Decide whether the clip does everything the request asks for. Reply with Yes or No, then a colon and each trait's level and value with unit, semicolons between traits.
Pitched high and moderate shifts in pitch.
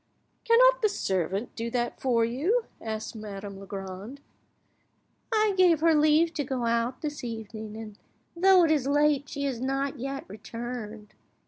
No: very high, 255 Hz; wide, 5.7 semitones